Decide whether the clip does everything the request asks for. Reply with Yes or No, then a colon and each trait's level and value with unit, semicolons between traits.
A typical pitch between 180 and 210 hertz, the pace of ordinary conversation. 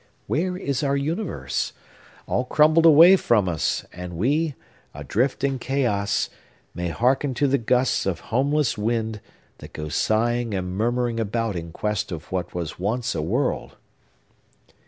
No: low, 120 Hz; average, 145 wpm